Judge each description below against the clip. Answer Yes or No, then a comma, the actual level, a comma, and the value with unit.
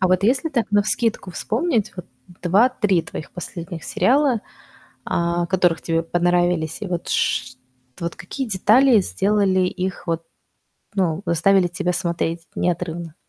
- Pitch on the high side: No, medium, 180 Hz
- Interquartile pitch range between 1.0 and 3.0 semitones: No, average, 3.4 semitones